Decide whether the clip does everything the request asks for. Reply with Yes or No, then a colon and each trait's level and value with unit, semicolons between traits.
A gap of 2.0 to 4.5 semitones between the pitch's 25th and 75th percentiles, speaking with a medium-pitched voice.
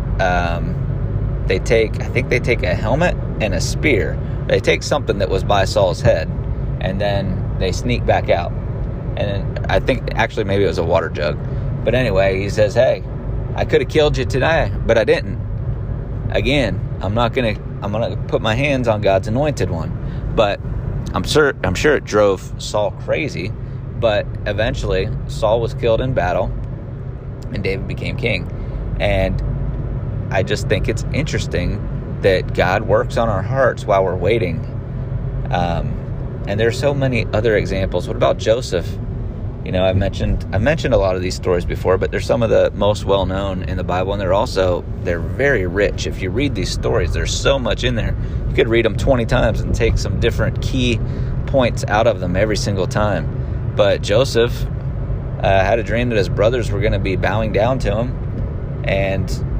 No: average, 3.9 semitones; low, 115 Hz